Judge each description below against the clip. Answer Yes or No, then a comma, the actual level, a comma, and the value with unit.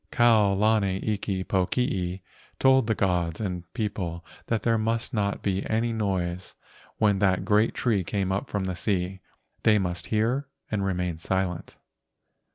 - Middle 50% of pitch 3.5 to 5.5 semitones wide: No, average, 3.1 semitones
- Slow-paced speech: No, average, 150 wpm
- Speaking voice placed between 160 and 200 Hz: No, low, 100 Hz